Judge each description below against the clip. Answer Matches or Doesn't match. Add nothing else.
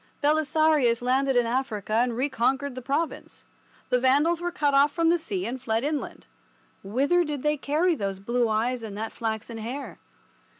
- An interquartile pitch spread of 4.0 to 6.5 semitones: Matches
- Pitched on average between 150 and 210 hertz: Doesn't match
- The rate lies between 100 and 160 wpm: Doesn't match